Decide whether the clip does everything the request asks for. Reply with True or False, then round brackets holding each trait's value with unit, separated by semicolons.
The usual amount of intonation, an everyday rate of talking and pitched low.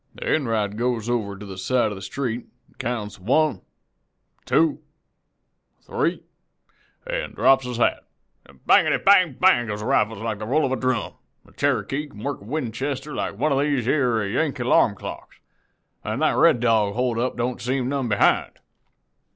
True (4.1 semitones; 160 wpm; 125 Hz)